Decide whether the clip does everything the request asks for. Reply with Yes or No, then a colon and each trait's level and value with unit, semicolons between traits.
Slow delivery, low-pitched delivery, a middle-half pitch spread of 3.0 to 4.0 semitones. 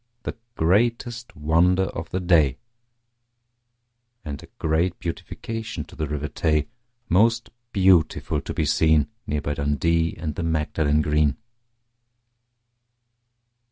Yes: slow, 115 wpm; very low, 80 Hz; average, 3.5 semitones